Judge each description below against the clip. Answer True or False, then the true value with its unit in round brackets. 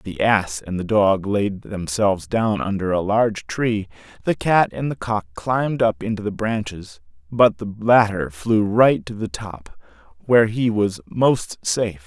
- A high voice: False (105 Hz)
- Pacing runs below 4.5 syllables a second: True (4.2 syllables/s)